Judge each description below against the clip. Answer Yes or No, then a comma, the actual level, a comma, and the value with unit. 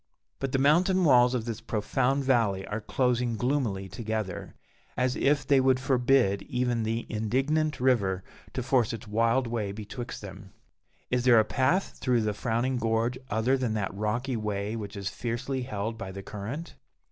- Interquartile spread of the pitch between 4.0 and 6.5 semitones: No, average, 3.6 semitones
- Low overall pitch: Yes, low, 120 Hz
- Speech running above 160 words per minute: Yes, average, 170 wpm